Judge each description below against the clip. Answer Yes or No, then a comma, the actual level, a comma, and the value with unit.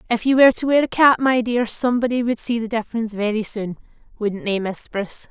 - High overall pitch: Yes, high, 230 Hz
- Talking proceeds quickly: Yes, fast, 215 wpm